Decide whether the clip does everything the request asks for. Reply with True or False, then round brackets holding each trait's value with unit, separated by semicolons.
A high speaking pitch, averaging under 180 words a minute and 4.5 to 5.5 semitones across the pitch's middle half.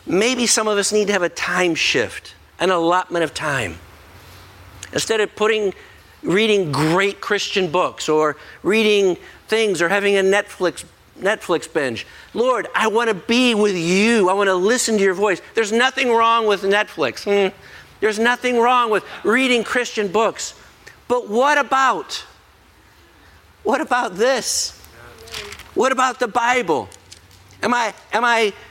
True (205 Hz; 145 wpm; 5.0 semitones)